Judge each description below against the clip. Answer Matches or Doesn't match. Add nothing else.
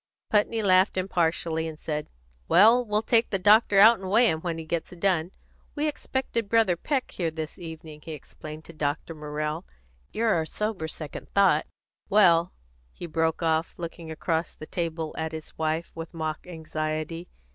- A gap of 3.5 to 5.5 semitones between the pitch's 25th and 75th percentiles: Matches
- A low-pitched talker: Doesn't match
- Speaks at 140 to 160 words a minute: Doesn't match